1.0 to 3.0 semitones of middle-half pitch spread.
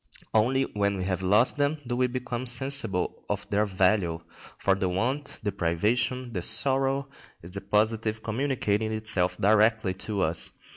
No: average, 4.4 semitones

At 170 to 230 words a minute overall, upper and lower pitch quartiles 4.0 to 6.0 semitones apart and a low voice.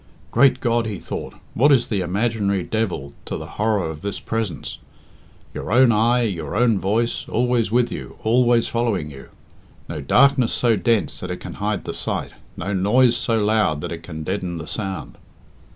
Yes: average, 180 wpm; average, 4.3 semitones; low, 110 Hz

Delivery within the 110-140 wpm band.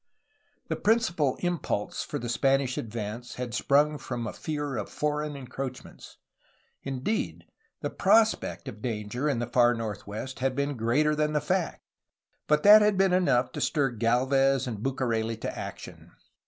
No: average, 155 wpm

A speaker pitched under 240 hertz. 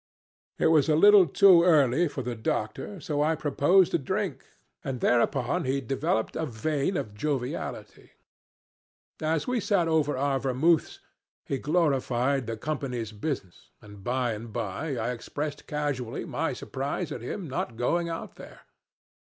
Yes: medium, 140 Hz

